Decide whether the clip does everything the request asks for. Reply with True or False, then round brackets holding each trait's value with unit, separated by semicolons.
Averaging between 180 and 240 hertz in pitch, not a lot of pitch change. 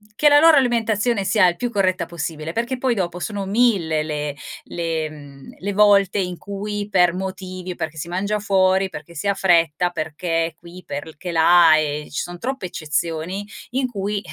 False (185 Hz; 3.8 semitones)